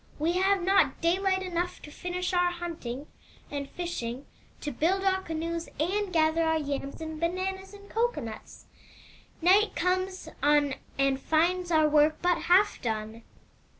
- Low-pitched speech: No, very high, 340 Hz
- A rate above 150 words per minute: No, average, 145 wpm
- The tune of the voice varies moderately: Yes, average, 3.9 semitones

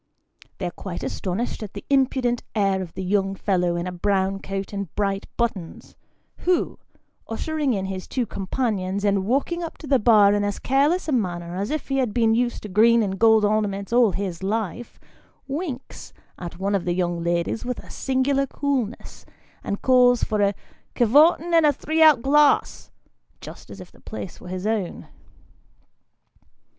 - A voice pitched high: Yes, high, 210 Hz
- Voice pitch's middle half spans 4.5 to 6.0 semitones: Yes, average, 5.2 semitones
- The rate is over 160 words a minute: Yes, average, 180 wpm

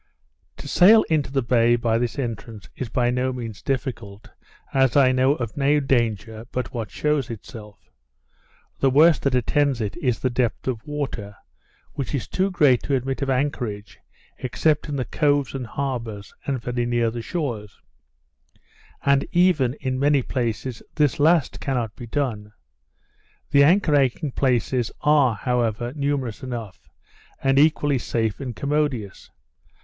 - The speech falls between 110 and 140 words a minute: No, average, 150 wpm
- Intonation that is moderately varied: Yes, average, 3.4 semitones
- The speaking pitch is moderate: No, low, 130 Hz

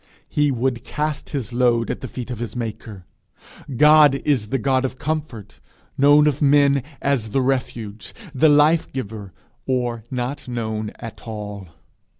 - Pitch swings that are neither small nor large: Yes, average, 4.0 semitones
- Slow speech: No, average, 150 wpm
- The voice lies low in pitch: Yes, low, 125 Hz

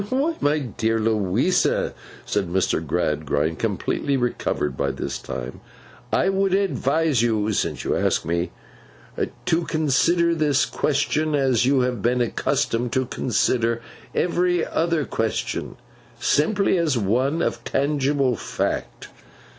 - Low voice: Yes, low, 130 Hz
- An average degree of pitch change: No, wide, 6.3 semitones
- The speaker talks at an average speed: No, slow, 125 wpm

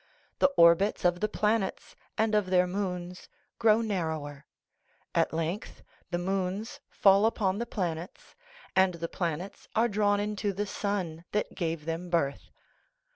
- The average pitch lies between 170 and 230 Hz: Yes, high, 190 Hz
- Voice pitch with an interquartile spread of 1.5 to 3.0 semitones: No, average, 3.5 semitones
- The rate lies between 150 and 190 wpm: No, average, 140 wpm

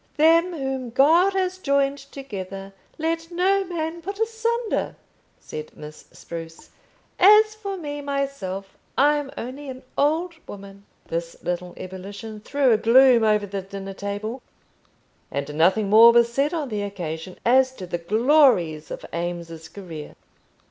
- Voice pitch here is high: Yes, high, 235 Hz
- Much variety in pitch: Yes, wide, 8.1 semitones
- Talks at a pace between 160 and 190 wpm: No, average, 140 wpm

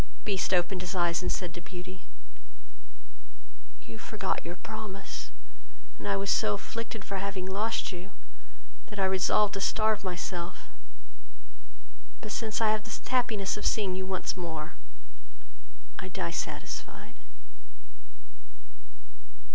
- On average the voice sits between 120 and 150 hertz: No, high, 190 Hz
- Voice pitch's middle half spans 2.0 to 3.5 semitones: Yes, average, 2.9 semitones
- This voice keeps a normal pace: No, slow, 125 wpm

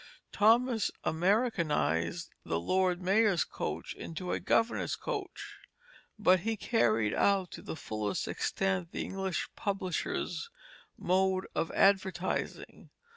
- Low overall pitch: No, medium, 185 Hz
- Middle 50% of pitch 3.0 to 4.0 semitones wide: No, average, 4.6 semitones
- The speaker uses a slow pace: Yes, slow, 110 wpm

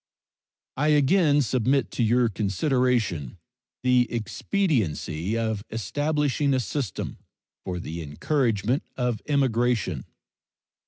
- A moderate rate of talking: No, slow, 95 wpm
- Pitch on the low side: Yes, low, 120 Hz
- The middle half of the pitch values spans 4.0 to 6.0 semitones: Yes, wide, 5.5 semitones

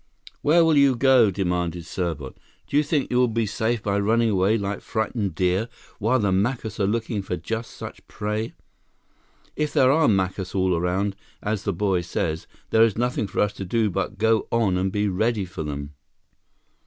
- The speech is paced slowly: No, average, 190 wpm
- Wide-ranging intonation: No, average, 3.6 semitones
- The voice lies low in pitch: Yes, low, 105 Hz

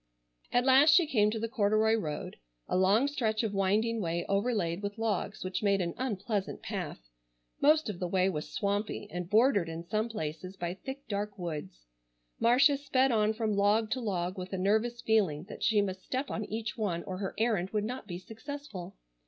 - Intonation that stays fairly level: No, average, 3.7 semitones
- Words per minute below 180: No, average, 190 wpm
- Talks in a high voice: Yes, high, 210 Hz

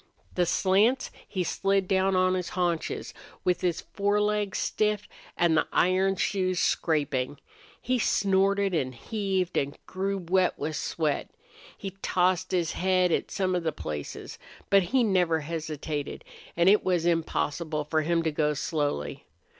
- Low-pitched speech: No, medium, 180 Hz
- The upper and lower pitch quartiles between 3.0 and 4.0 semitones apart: Yes, average, 3.3 semitones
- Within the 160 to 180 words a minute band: No, average, 145 wpm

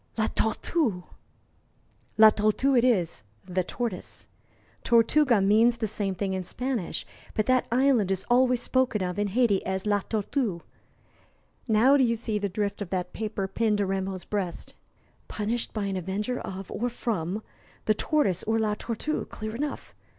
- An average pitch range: Yes, average, 3.7 semitones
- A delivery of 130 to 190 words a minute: Yes, average, 160 wpm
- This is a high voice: Yes, high, 215 Hz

